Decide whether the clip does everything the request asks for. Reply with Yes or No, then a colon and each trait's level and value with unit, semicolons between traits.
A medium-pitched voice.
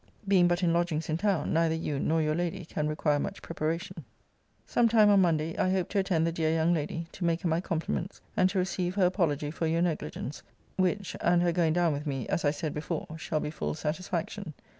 Yes: medium, 165 Hz